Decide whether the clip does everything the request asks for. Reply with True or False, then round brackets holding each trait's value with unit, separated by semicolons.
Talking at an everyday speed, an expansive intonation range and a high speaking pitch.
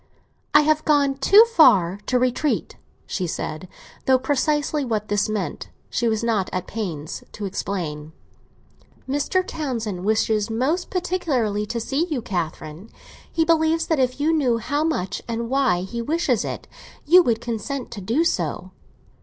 True (155 wpm; 6.4 semitones; 240 Hz)